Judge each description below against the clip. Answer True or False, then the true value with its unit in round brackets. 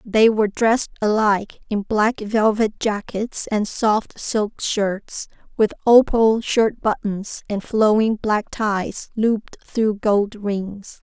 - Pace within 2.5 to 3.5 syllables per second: True (3.4 syllables/s)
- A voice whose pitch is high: True (215 Hz)